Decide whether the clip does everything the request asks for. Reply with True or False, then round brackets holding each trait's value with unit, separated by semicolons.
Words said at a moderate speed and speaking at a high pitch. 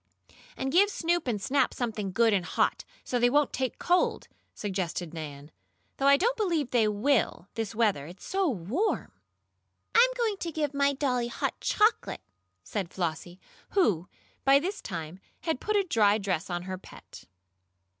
True (165 wpm; 240 Hz)